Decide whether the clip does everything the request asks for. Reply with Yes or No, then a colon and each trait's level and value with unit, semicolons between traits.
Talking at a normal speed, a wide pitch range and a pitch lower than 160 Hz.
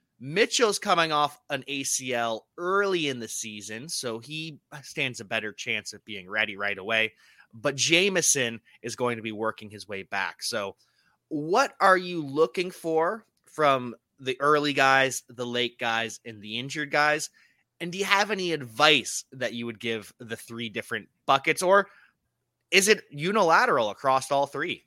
Yes: average, 165 wpm; wide, 5.7 semitones; low, 135 Hz